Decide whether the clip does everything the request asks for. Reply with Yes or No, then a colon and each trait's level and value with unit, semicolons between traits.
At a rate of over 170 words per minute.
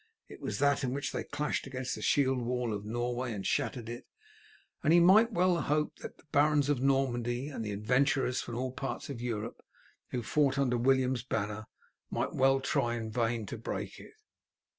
Yes: average, 190 wpm